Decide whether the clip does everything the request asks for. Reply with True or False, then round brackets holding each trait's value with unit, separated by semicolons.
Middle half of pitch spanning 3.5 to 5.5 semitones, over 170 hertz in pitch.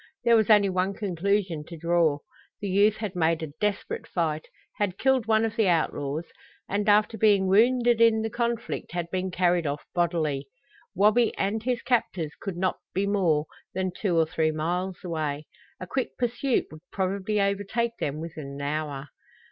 True (4.7 semitones; 190 Hz)